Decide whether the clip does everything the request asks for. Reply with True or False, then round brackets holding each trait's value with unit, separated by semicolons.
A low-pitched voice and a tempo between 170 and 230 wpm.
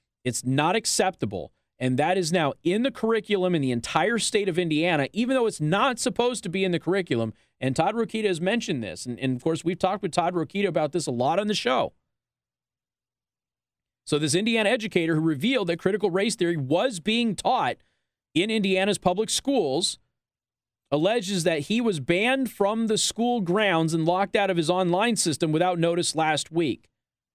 False (185 Hz; 185 wpm)